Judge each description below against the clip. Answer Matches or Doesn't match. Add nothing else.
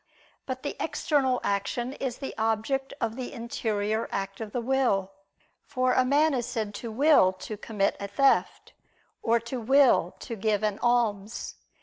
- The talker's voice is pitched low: Doesn't match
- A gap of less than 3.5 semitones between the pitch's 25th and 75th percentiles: Doesn't match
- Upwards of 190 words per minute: Doesn't match